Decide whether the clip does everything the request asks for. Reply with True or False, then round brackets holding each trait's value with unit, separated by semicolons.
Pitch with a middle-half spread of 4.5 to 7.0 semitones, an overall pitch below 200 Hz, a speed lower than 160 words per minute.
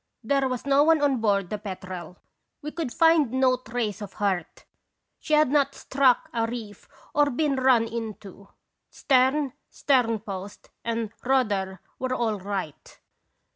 False (5.0 semitones; 235 Hz; 140 wpm)